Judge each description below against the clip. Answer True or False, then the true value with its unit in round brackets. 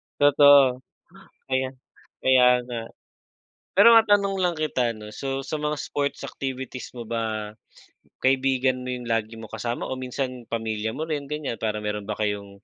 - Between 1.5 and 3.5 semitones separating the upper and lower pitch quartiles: False (3.9 semitones)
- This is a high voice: False (125 Hz)